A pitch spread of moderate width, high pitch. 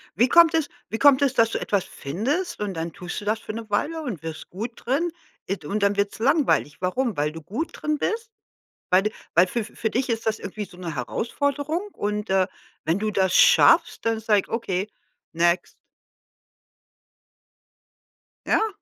No: wide, 6.6 semitones; high, 215 Hz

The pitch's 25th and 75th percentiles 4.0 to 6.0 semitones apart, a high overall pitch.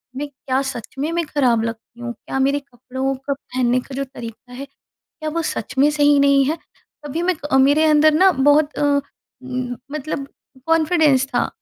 No: average, 2.8 semitones; very high, 275 Hz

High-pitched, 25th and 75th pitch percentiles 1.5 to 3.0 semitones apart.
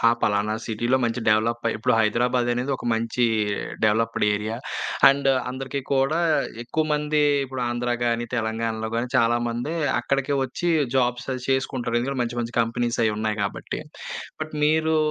No: low, 120 Hz; average, 2.7 semitones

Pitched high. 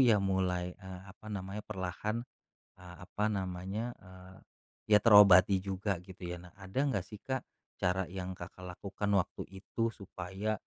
No: very low, 95 Hz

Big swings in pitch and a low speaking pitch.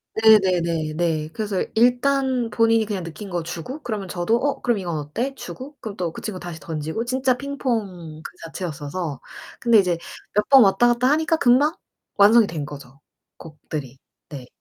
No: wide, 6.7 semitones; high, 200 Hz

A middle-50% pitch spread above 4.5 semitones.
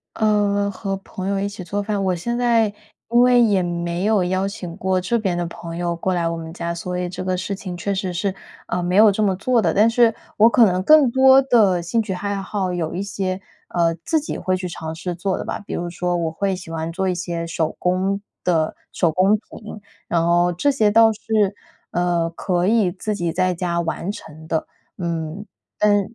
No: average, 3.1 semitones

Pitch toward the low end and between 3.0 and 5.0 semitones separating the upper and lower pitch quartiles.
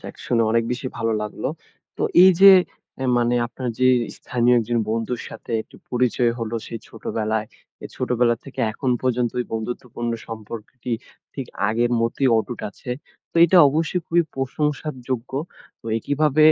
No: low, 120 Hz; narrow, 2.5 semitones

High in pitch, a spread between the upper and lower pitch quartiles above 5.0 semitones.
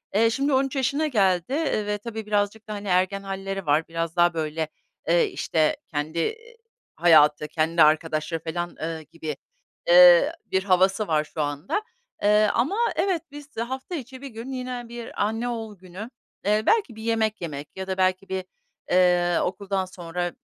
Yes: high, 195 Hz; wide, 5.5 semitones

